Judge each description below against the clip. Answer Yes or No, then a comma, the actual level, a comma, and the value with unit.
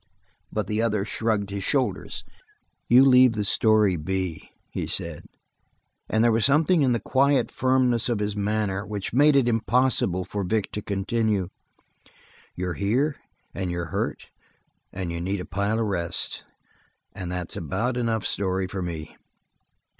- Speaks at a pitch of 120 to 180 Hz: No, low, 105 Hz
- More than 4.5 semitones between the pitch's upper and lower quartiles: No, average, 4.0 semitones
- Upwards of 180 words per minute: No, average, 150 wpm